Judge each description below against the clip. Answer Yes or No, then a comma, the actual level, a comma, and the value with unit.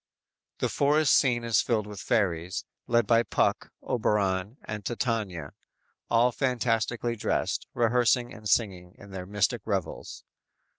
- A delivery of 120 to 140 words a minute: Yes, slow, 135 wpm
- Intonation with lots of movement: No, average, 3.4 semitones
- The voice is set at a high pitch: No, low, 110 Hz